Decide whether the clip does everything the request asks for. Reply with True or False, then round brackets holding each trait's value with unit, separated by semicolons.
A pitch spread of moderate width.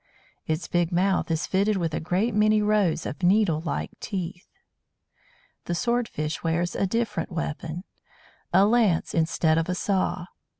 True (3.9 semitones)